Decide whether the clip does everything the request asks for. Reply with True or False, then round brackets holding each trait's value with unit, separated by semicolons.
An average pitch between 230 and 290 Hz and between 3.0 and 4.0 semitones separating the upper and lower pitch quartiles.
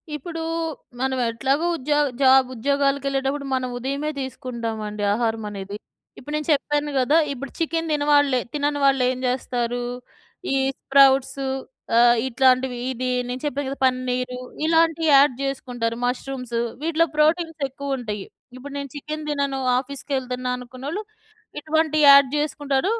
False (270 Hz; 2.6 semitones)